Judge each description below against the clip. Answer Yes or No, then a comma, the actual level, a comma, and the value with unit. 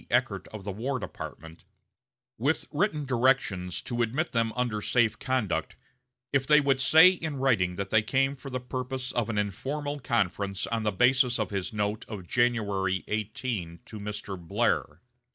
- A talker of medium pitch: No, low, 115 Hz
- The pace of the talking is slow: No, average, 165 wpm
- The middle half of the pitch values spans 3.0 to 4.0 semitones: No, average, 4.6 semitones